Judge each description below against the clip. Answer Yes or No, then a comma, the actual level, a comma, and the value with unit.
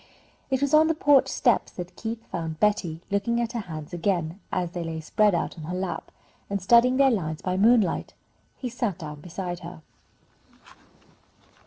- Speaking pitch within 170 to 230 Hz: Yes, medium, 185 Hz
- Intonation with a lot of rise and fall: Yes, wide, 5.8 semitones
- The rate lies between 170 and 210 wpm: Yes, average, 175 wpm